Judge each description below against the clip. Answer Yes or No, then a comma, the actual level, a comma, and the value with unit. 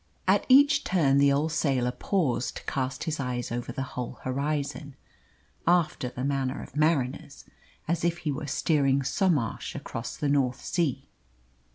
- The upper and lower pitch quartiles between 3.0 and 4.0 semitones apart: Yes, average, 3.5 semitones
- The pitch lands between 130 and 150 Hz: Yes, medium, 140 Hz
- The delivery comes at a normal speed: Yes, average, 155 wpm